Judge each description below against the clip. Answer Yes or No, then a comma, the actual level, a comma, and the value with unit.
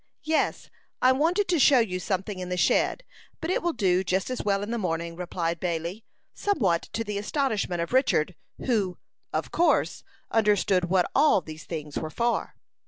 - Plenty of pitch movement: Yes, wide, 6.2 semitones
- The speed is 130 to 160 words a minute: No, average, 175 wpm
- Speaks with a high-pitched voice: Yes, high, 195 Hz